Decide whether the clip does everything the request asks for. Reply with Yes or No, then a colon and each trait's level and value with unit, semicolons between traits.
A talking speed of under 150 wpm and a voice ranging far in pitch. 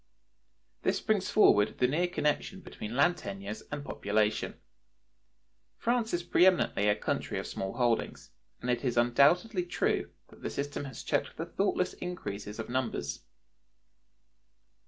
Yes: average, 140 wpm; wide, 8.2 semitones